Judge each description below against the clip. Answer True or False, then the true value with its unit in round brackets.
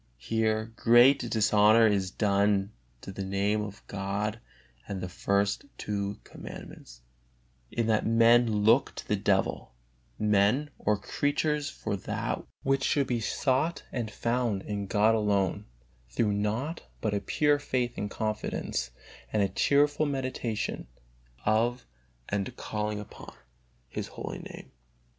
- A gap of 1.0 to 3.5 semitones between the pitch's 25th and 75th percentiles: True (3.1 semitones)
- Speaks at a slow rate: True (130 wpm)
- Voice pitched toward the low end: True (110 Hz)